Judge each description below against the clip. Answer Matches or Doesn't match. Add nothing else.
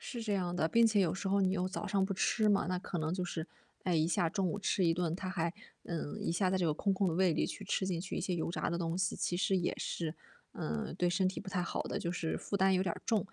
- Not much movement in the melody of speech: Matches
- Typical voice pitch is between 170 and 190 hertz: Matches